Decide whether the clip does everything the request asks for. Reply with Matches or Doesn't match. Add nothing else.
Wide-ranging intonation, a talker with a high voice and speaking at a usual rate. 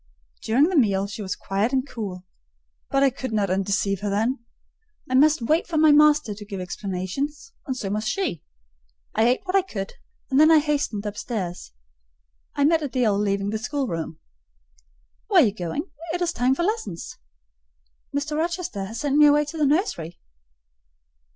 Matches